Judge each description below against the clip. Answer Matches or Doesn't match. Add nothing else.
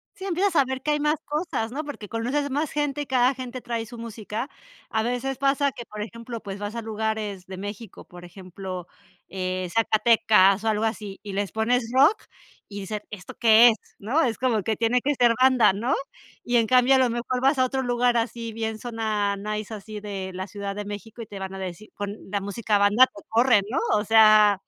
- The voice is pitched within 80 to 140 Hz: Doesn't match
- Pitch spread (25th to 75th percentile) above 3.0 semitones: Matches